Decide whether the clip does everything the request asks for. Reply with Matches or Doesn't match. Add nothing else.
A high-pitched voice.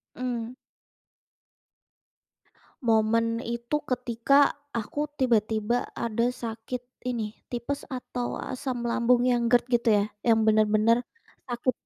Matches